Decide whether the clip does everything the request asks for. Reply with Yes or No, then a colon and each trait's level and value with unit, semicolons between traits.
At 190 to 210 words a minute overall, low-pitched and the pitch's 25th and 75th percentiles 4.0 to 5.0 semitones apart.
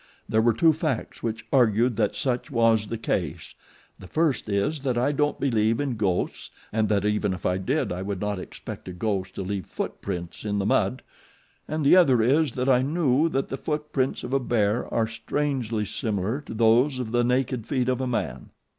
Yes: average, 200 wpm; low, 115 Hz; average, 4.4 semitones